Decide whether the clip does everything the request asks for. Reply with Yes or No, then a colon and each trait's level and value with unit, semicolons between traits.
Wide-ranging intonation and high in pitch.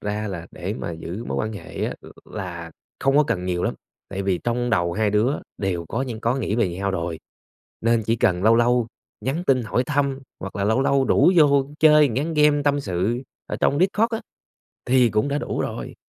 No: wide, 6.0 semitones; low, 115 Hz